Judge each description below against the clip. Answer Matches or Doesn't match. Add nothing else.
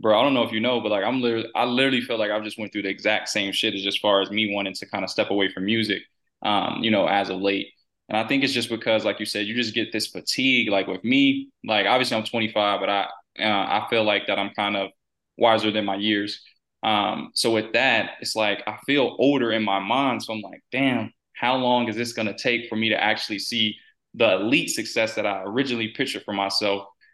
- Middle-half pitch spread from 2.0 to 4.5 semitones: Matches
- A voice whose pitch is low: Matches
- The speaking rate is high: Matches